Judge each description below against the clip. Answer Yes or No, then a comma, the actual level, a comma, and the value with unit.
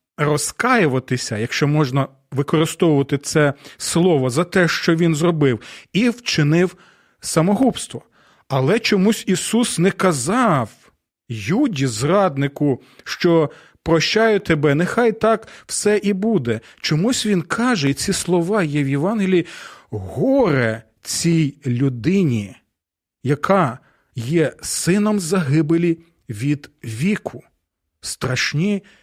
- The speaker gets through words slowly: Yes, slow, 100 wpm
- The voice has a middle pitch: Yes, medium, 165 Hz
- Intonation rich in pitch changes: Yes, wide, 5.9 semitones